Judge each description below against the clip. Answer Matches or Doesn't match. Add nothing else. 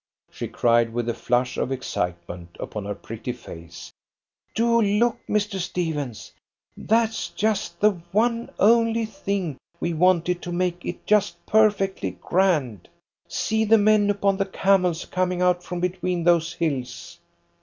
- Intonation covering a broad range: Matches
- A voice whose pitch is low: Doesn't match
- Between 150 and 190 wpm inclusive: Doesn't match